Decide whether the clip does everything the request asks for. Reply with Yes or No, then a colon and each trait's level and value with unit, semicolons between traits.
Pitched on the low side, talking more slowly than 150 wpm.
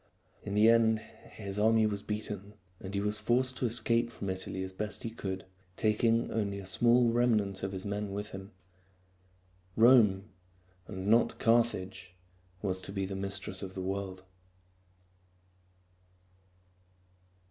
Yes: low, 105 Hz; average, 140 wpm